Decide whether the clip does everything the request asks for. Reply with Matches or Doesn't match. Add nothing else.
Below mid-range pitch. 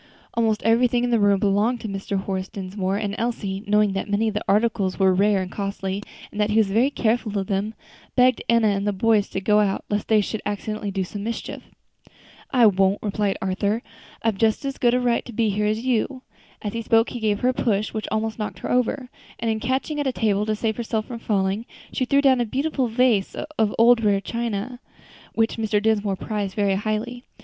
Doesn't match